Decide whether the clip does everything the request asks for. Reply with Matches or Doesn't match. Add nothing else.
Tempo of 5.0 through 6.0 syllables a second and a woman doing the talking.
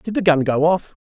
Doesn't match